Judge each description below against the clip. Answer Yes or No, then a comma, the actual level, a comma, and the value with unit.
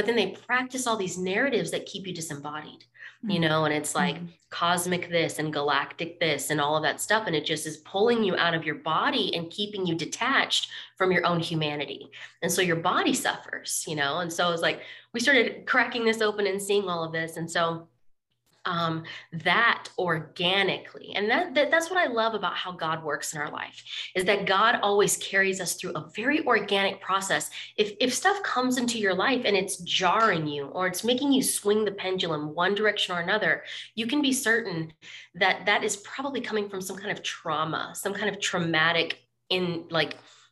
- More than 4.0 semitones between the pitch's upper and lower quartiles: Yes, average, 4.4 semitones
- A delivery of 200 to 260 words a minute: Yes, fast, 205 wpm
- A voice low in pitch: No, medium, 180 Hz